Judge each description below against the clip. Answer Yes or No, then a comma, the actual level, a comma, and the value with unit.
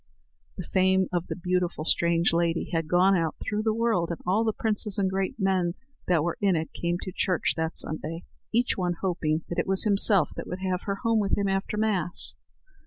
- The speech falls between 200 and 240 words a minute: Yes, fast, 205 wpm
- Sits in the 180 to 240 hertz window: Yes, medium, 185 Hz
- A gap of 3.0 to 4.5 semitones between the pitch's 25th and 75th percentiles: No, narrow, 2.6 semitones